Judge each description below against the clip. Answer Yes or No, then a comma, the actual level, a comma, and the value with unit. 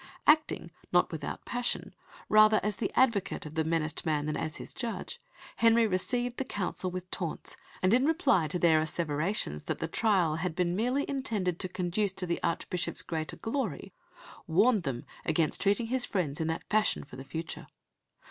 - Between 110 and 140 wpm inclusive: No, average, 175 wpm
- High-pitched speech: No, medium, 180 Hz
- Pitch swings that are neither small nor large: No, wide, 5.8 semitones